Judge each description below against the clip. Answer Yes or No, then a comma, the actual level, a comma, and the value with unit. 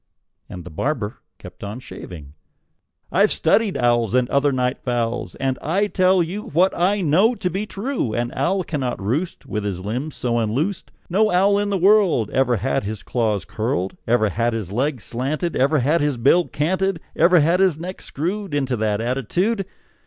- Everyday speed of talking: Yes, average, 180 wpm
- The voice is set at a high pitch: No, medium, 140 Hz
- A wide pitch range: Yes, wide, 7.7 semitones